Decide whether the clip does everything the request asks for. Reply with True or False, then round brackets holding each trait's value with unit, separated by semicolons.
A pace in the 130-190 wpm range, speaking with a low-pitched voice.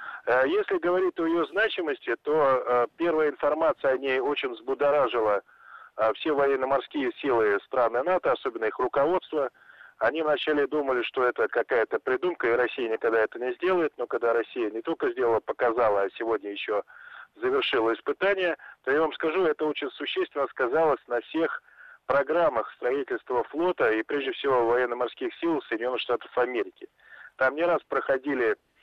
False (145 wpm; 290 Hz)